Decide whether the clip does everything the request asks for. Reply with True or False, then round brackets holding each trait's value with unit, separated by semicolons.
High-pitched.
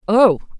True (215 Hz)